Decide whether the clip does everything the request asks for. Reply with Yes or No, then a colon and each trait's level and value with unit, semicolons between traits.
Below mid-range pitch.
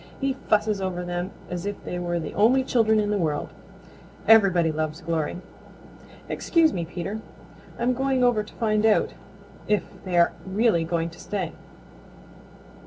No: high, 195 Hz